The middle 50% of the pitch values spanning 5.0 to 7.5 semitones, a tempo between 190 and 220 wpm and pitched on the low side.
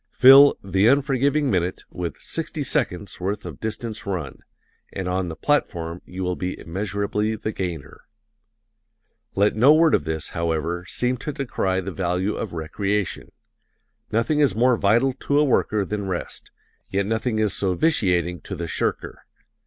No: wide, 5.5 semitones; average, 155 wpm; low, 100 Hz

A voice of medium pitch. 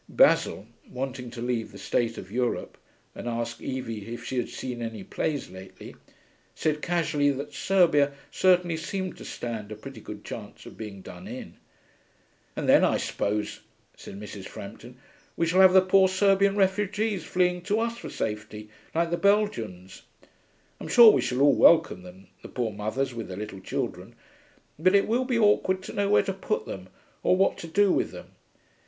Yes: medium, 145 Hz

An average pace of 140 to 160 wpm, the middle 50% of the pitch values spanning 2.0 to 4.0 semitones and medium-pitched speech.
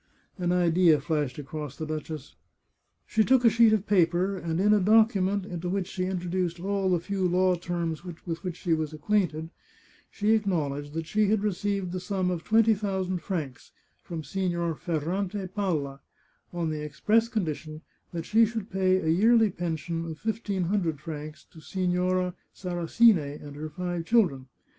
No: average, 175 wpm; average, 3.6 semitones; medium, 180 Hz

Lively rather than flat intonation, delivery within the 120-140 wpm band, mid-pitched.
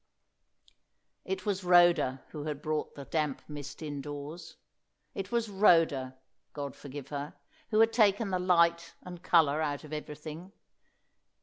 No: average, 3.8 semitones; slow, 135 wpm; medium, 155 Hz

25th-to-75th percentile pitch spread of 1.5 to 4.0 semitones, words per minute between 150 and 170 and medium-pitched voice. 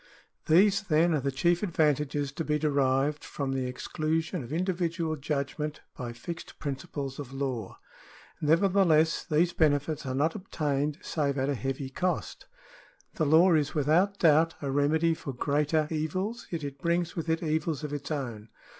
Yes: average, 3.0 semitones; average, 160 wpm; medium, 150 Hz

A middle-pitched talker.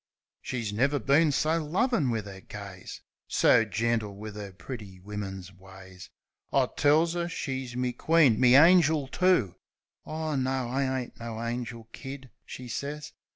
No: low, 125 Hz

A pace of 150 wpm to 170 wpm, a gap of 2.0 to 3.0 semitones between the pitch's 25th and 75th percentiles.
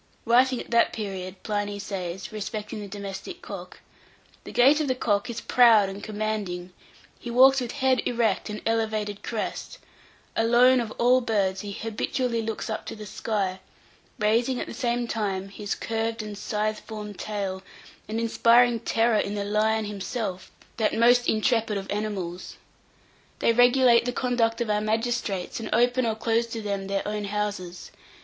Yes: average, 165 wpm; narrow, 2.5 semitones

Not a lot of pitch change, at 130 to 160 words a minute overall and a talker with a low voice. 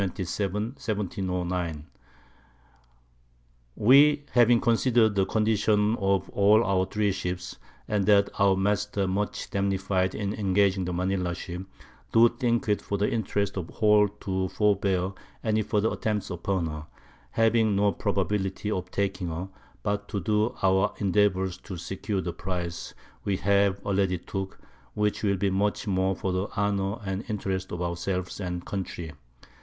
Yes: narrow, 2.0 semitones; average, 150 wpm; low, 100 Hz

